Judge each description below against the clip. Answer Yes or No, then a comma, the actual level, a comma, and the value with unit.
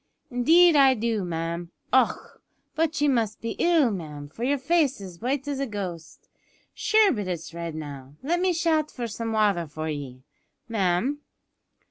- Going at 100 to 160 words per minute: No, average, 170 wpm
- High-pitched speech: Yes, high, 225 Hz